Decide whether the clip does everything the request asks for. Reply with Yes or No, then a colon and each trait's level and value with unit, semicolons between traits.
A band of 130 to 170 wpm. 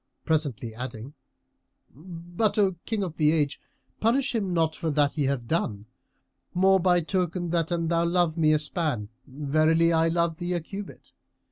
Yes: average, 165 wpm